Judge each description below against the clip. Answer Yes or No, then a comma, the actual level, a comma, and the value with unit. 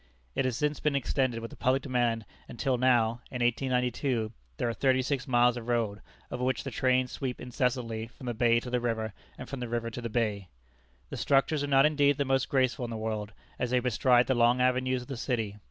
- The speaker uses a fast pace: Yes, fast, 225 wpm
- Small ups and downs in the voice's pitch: Yes, narrow, 1.9 semitones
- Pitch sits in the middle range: No, low, 125 Hz